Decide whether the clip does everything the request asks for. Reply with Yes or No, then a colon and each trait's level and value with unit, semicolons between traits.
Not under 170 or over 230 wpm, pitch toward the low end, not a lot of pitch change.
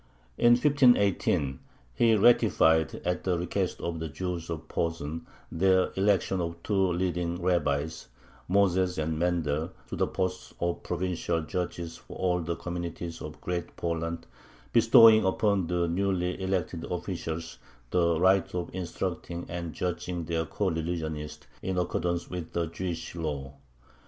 No: slow, 135 wpm; very low, 85 Hz; narrow, 2.1 semitones